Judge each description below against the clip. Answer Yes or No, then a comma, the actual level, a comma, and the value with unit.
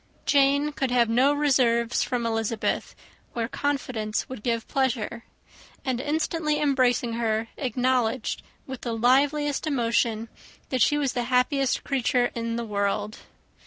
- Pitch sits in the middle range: No, very high, 250 Hz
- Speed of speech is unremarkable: No, slow, 130 wpm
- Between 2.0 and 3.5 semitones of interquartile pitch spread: Yes, average, 3.1 semitones